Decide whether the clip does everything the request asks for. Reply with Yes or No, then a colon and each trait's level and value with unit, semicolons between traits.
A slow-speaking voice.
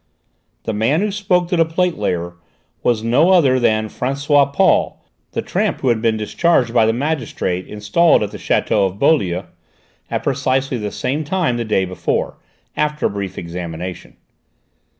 No: average, 165 wpm